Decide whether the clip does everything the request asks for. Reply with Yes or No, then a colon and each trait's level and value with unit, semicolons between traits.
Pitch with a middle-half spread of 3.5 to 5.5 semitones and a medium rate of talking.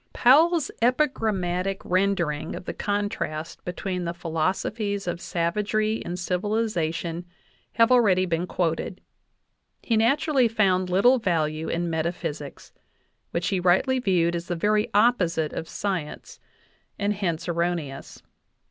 No: average, 4.1 semitones; slow, 120 wpm